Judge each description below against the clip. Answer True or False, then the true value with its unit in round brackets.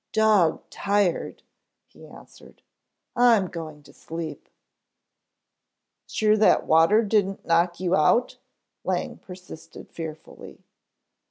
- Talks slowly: True (95 wpm)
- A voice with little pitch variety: False (4.4 semitones)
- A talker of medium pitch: True (180 Hz)